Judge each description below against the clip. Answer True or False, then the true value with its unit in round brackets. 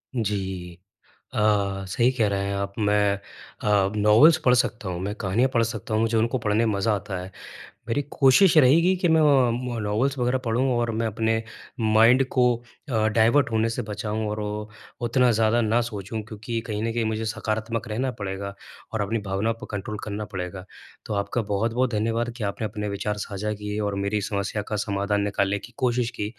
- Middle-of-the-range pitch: False (110 Hz)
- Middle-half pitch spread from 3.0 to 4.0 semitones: False (2.4 semitones)